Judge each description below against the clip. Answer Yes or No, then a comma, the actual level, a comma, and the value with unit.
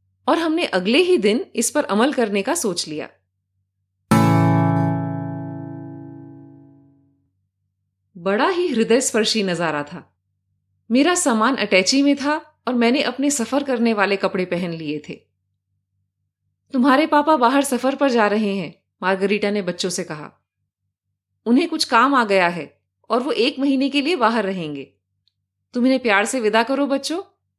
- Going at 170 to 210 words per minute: No, average, 145 wpm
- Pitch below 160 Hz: No, high, 190 Hz